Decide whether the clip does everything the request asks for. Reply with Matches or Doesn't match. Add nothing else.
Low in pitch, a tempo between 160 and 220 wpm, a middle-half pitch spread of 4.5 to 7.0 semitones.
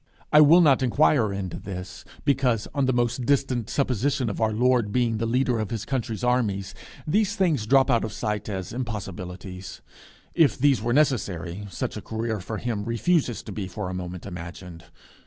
Matches